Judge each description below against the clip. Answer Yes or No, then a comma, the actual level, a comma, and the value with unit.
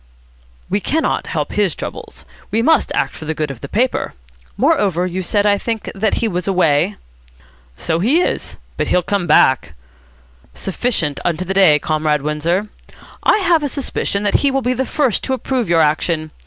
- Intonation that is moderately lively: No, wide, 6.7 semitones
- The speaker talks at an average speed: Yes, average, 180 wpm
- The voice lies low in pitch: No, high, 190 Hz